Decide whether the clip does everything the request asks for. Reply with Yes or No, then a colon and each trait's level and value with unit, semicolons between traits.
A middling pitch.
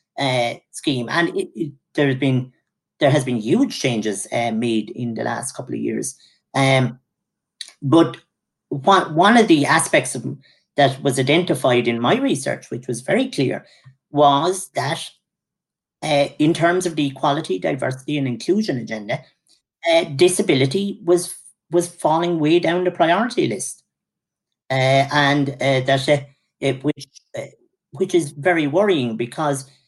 Yes: medium, 145 Hz